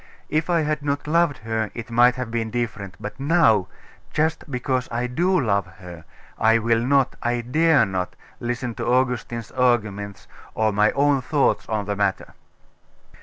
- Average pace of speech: Yes, average, 165 wpm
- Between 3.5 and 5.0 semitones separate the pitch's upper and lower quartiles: Yes, average, 4.4 semitones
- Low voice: Yes, low, 120 Hz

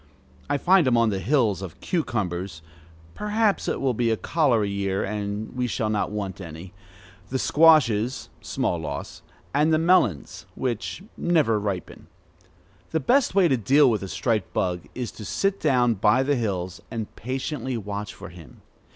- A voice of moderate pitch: No, low, 115 Hz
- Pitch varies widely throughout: Yes, wide, 6.3 semitones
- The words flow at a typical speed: Yes, average, 165 wpm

